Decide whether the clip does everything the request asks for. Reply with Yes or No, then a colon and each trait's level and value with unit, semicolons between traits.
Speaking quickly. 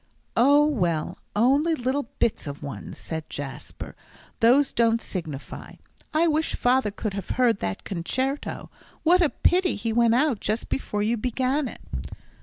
No: average, 150 wpm